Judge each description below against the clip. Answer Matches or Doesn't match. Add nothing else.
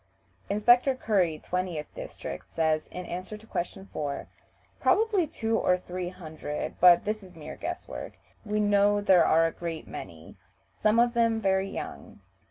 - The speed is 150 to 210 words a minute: Matches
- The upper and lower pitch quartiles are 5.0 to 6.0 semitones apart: Doesn't match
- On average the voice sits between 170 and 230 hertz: Matches